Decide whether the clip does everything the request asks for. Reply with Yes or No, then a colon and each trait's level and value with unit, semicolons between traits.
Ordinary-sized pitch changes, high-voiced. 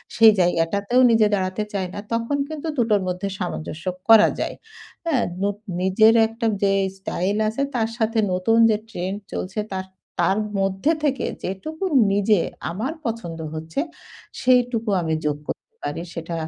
Yes: average, 3.7 semitones; high, 205 Hz